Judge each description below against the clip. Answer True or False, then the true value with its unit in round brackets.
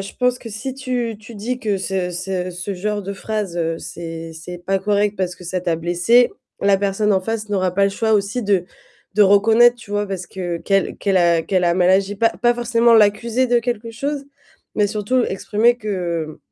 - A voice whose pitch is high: True (200 Hz)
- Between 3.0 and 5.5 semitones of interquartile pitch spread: True (3.7 semitones)